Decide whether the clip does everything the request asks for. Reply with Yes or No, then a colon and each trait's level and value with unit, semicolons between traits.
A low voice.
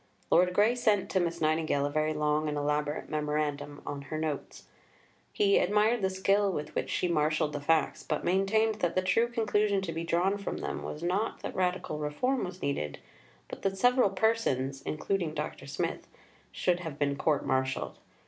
No: medium, 170 Hz